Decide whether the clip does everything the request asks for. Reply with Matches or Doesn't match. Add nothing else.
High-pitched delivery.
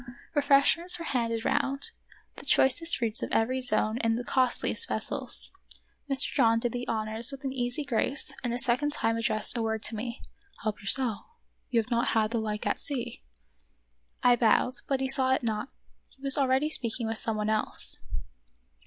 Matches